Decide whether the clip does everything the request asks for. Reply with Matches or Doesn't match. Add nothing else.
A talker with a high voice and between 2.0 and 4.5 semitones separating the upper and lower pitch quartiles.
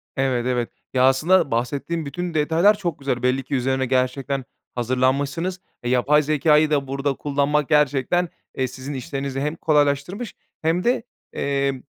Doesn't match